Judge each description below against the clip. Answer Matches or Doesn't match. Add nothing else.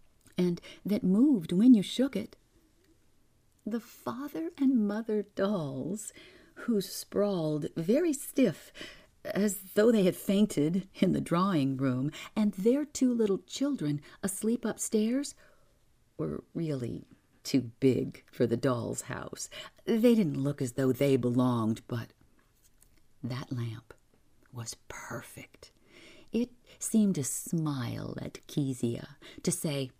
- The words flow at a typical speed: Doesn't match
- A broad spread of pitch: Matches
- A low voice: Doesn't match